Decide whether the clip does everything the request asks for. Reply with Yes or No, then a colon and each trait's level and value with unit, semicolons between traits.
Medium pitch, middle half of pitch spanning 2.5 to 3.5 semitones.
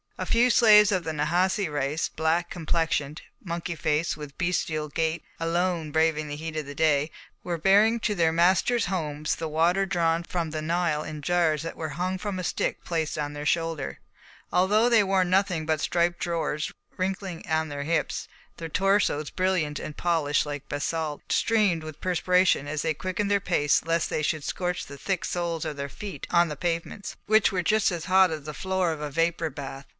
Yes: medium, 165 Hz; average, 3.1 semitones